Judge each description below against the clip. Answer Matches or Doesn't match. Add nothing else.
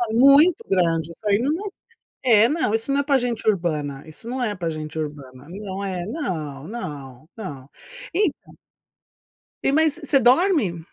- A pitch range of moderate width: Doesn't match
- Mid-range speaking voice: Doesn't match